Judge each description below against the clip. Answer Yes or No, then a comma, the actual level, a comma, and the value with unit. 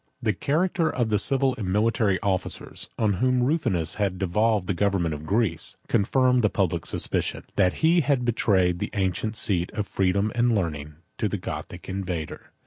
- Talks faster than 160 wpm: Yes, average, 175 wpm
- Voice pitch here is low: Yes, low, 100 Hz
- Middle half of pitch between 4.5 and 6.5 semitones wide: Yes, average, 4.8 semitones